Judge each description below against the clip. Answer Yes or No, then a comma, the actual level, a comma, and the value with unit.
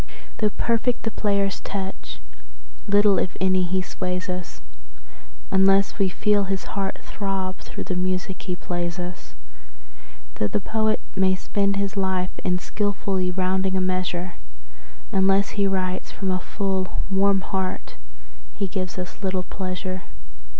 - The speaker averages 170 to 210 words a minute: No, average, 140 wpm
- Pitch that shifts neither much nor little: No, narrow, 1.4 semitones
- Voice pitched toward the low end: No, high, 190 Hz